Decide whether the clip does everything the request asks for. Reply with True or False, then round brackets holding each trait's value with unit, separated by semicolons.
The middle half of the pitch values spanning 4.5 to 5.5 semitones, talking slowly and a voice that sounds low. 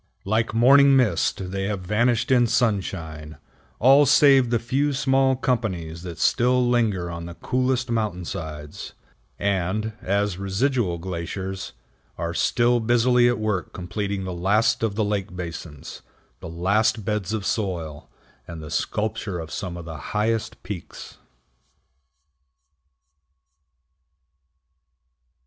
True (5.2 semitones; 120 wpm; 105 Hz)